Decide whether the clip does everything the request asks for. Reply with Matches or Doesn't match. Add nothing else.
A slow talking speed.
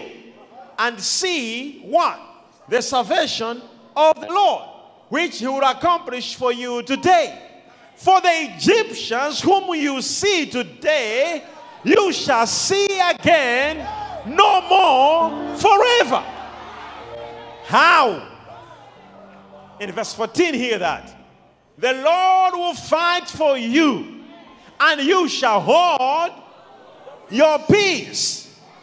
Matches